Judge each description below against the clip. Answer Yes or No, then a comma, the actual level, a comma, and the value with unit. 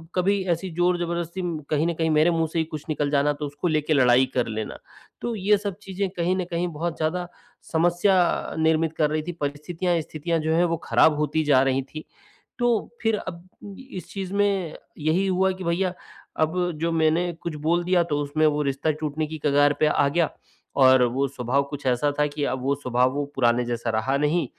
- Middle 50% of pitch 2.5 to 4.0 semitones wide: Yes, average, 3.5 semitones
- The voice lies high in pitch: No, medium, 160 Hz